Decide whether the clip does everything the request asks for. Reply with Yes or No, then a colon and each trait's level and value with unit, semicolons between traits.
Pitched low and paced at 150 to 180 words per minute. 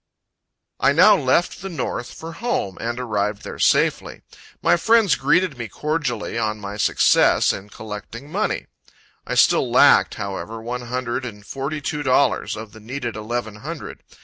Yes: low, 125 Hz; average, 155 wpm